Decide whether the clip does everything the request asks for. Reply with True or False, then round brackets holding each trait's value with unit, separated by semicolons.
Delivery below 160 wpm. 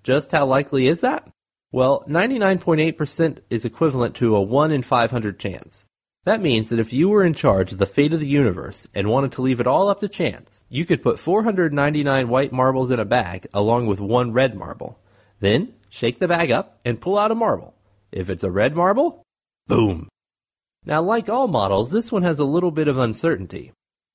False (200 wpm)